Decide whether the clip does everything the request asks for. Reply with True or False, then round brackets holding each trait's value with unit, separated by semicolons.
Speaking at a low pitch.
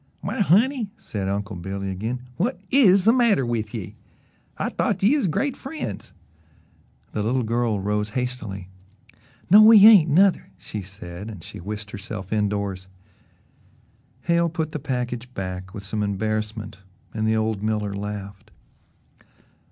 True (110 Hz)